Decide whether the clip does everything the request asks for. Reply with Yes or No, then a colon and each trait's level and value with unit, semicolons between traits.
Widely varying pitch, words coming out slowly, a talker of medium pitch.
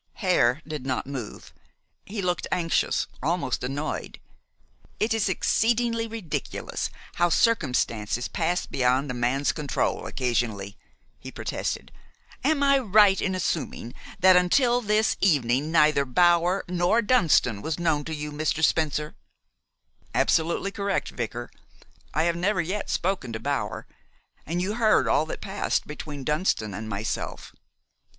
Yes: wide, 6.5 semitones; slow, 130 wpm; medium, 165 Hz